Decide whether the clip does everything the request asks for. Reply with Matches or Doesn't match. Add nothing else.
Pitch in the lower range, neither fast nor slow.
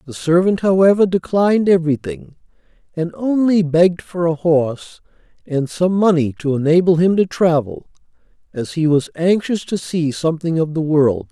Doesn't match